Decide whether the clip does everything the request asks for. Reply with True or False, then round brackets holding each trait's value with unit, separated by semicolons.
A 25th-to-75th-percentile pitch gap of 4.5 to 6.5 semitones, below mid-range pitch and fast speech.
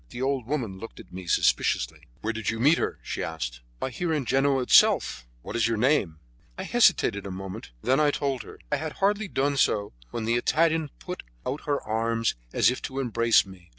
True (5.0 semitones; 120 Hz; 215 wpm)